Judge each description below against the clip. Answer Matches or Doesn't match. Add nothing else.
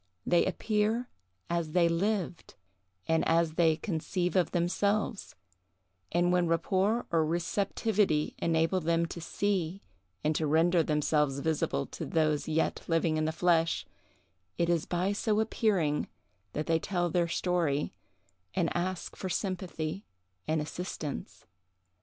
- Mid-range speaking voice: Matches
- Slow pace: Matches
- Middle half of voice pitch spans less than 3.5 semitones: Matches